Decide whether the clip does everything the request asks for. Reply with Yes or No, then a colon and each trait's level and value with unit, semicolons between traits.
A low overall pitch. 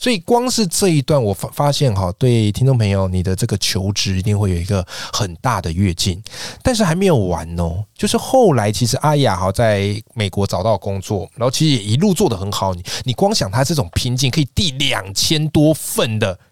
Yes: low, 115 Hz